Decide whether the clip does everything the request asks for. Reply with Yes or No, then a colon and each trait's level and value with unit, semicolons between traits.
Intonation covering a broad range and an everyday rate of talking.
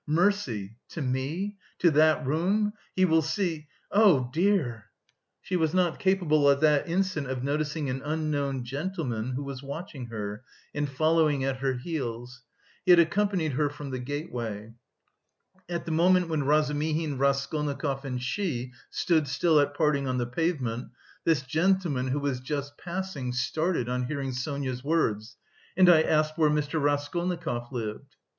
No: average, 4.2 semitones; average, 150 wpm